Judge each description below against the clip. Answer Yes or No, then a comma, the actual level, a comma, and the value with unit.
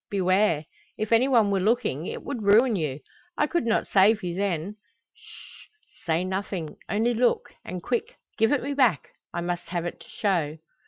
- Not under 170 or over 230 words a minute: Yes, average, 180 wpm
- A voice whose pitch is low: No, high, 200 Hz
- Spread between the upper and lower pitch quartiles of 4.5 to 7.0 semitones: Yes, average, 5.0 semitones